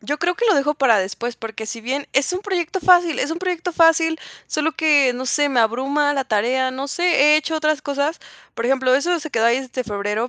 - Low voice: No, very high, 285 Hz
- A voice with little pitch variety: No, average, 4.6 semitones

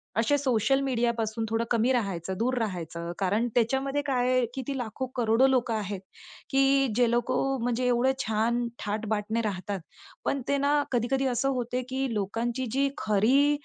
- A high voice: Yes, high, 240 Hz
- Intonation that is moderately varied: Yes, average, 3.4 semitones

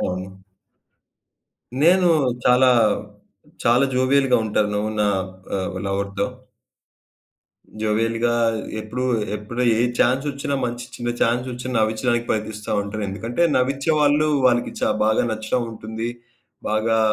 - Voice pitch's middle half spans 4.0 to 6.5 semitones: No, average, 2.9 semitones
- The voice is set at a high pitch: No, low, 115 Hz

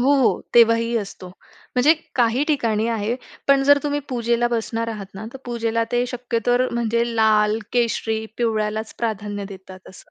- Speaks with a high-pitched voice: Yes, high, 230 Hz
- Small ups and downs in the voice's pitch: Yes, narrow, 2.0 semitones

